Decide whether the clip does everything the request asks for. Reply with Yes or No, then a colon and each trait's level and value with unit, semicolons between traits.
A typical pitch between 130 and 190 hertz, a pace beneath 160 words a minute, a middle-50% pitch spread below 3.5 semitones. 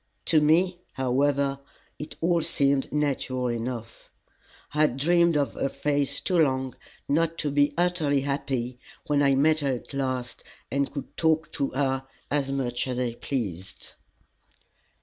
Yes: medium, 140 Hz; average, 150 wpm; narrow, 2.5 semitones